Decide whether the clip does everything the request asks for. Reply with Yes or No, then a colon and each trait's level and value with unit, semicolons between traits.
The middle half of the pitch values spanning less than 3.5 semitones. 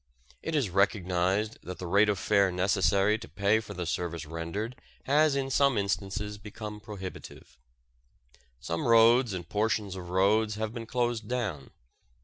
Yes: average, 3.1 semitones